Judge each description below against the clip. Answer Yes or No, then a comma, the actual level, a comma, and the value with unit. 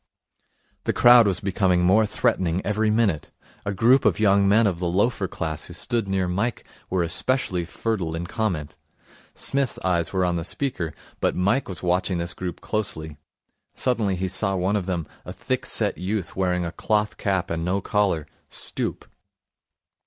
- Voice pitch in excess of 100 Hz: No, very low, 95 Hz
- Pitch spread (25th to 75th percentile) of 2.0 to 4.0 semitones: Yes, average, 3.3 semitones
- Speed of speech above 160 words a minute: Yes, average, 170 wpm